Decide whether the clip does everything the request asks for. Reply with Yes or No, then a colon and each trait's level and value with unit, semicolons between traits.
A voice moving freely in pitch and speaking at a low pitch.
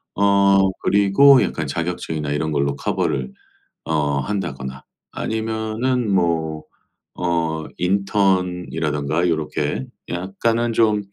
No: average, 4.7 semitones; very low, 90 Hz